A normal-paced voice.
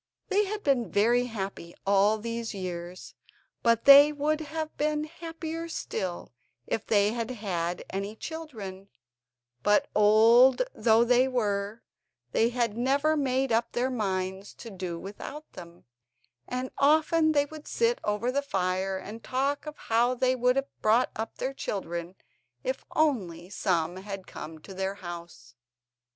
Yes: average, 145 wpm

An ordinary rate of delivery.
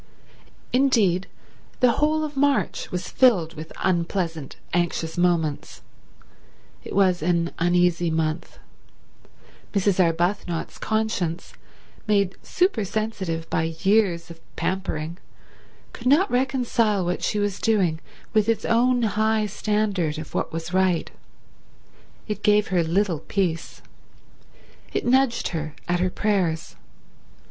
No: slow, 115 wpm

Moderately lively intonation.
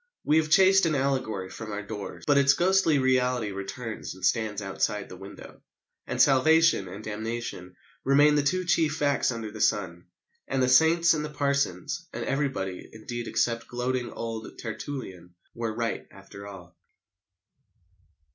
No: wide, 5.7 semitones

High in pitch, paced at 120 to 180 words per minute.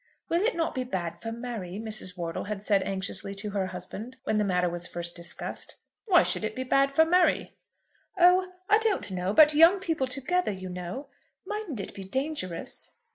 No: high, 220 Hz; average, 190 wpm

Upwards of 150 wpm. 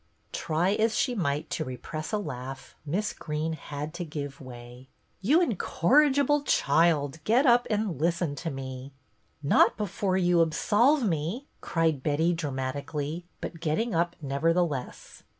No: average, 145 wpm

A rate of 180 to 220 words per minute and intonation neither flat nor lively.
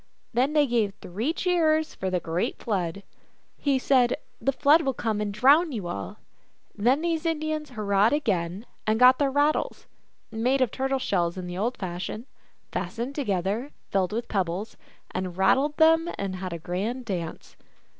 No: average, 185 wpm; wide, 6.7 semitones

